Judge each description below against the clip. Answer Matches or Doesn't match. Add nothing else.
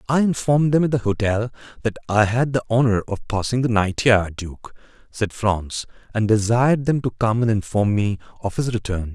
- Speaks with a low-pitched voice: Matches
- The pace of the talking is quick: Doesn't match